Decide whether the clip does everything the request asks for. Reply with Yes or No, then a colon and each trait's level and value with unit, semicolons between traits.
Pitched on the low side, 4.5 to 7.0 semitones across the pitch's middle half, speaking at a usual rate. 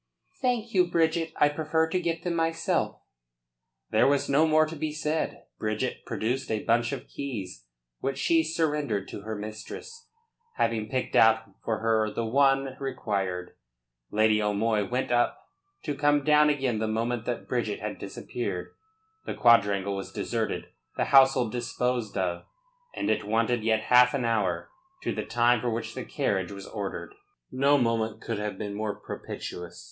Yes: low, 120 Hz; average, 5.3 semitones; average, 160 wpm